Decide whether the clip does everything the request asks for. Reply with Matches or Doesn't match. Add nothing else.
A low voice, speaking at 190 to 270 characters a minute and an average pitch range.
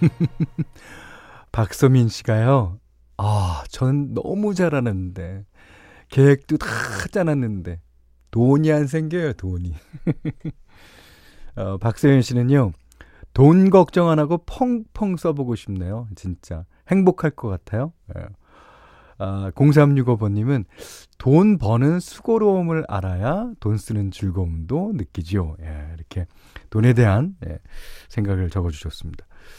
Doesn't match